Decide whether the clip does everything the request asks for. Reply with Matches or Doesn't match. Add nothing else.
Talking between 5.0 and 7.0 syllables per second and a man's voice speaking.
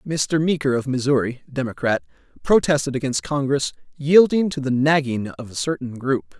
Matches